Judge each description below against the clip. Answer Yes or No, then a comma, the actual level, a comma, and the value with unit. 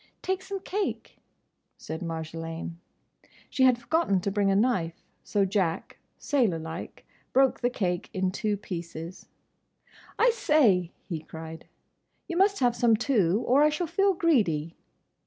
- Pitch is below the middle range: No, high, 205 Hz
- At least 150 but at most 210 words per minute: No, average, 140 wpm